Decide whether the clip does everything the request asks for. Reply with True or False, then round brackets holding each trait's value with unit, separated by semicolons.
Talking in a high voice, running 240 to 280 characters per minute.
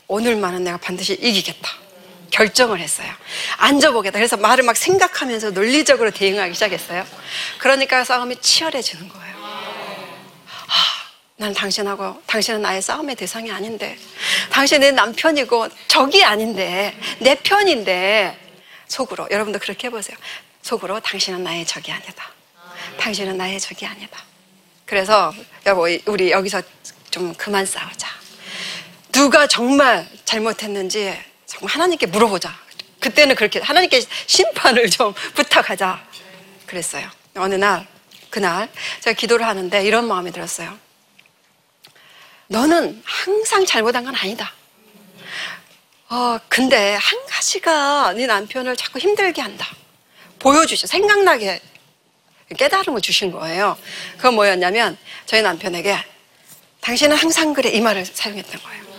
False (215 Hz; 295 characters per minute)